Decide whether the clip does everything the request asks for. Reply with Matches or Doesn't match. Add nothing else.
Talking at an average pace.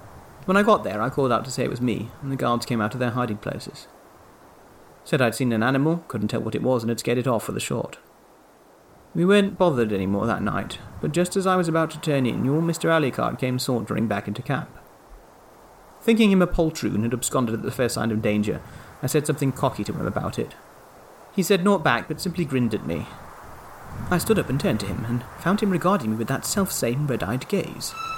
Doesn't match